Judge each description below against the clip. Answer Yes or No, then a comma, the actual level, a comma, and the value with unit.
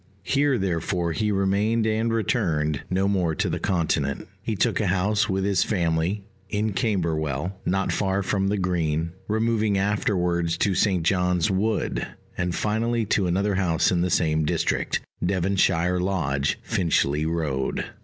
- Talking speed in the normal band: Yes, average, 145 wpm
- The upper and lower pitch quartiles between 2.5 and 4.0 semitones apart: Yes, average, 3.6 semitones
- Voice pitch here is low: Yes, very low, 95 Hz